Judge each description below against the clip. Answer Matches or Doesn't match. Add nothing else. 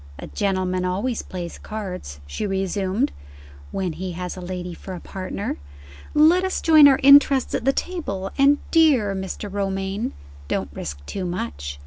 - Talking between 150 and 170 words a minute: Matches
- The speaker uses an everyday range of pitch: Doesn't match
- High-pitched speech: Matches